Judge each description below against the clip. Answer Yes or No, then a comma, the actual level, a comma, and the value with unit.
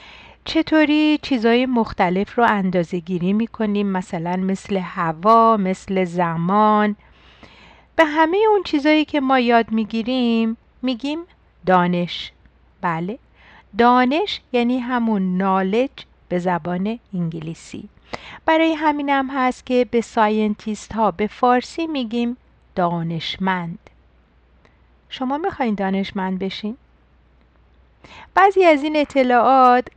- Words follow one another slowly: Yes, slow, 100 wpm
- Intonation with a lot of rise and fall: Yes, wide, 5.9 semitones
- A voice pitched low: No, high, 215 Hz